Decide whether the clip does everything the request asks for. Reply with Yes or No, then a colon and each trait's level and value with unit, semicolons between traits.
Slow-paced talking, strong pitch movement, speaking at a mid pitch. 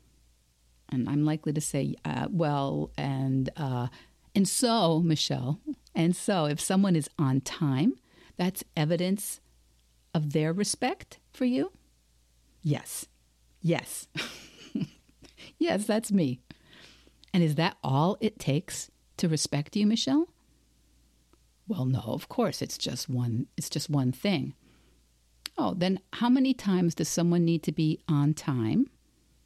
Yes: slow, 130 wpm; wide, 7.0 semitones; medium, 150 Hz